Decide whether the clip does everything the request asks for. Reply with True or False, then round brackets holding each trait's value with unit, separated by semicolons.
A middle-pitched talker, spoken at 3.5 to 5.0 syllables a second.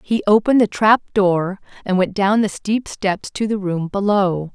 False (200 Hz; 4.5 syllables/s)